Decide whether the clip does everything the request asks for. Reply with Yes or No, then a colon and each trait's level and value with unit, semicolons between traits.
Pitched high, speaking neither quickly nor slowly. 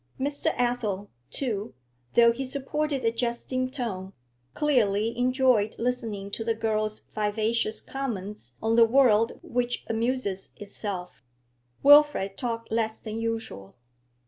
No: high, 230 Hz; slow, 120 wpm